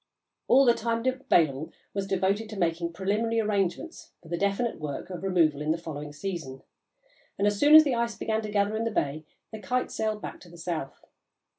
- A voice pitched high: Yes, high, 195 Hz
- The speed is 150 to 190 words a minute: No, fast, 205 wpm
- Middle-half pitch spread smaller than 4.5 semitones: No, average, 5.2 semitones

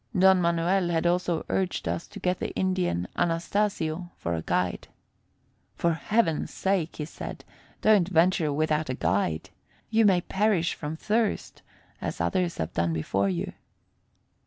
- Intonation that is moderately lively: Yes, average, 4.3 semitones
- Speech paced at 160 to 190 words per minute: No, average, 145 wpm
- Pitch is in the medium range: Yes, medium, 170 Hz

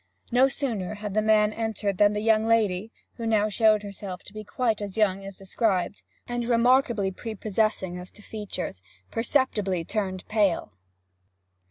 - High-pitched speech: Yes, high, 210 Hz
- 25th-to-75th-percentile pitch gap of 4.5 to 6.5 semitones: No, narrow, 2.5 semitones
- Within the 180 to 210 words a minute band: No, average, 160 wpm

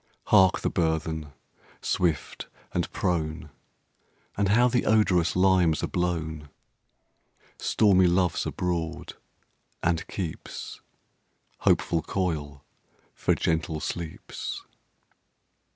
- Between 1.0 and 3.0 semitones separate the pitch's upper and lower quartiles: Yes, average, 2.7 semitones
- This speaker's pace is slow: Yes, slow, 90 wpm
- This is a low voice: Yes, very low, 85 Hz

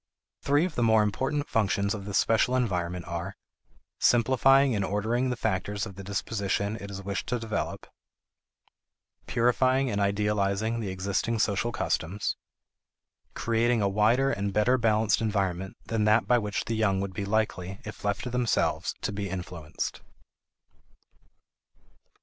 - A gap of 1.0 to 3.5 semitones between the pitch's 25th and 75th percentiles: Yes, average, 3.0 semitones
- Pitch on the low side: Yes, low, 105 Hz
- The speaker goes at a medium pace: Yes, average, 145 wpm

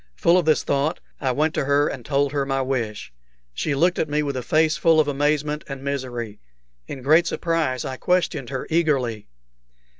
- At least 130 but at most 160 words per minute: No, average, 190 wpm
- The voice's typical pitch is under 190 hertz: Yes, medium, 140 Hz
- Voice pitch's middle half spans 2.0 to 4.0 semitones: Yes, average, 2.9 semitones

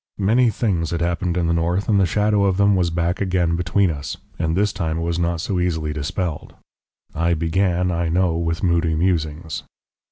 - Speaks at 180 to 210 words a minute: Yes, average, 195 wpm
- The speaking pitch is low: Yes, very low, 85 Hz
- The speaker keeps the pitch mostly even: Yes, narrow, 2.2 semitones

